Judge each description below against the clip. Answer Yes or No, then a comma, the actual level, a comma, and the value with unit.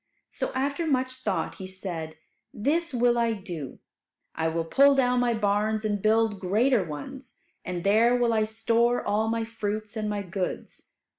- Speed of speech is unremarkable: Yes, average, 165 wpm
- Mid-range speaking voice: No, high, 220 Hz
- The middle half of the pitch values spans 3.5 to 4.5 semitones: Yes, average, 3.9 semitones